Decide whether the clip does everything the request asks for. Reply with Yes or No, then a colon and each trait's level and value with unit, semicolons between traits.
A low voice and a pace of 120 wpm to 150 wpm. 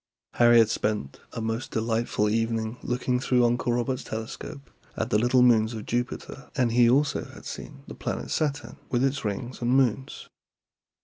No: low, 120 Hz; average, 170 wpm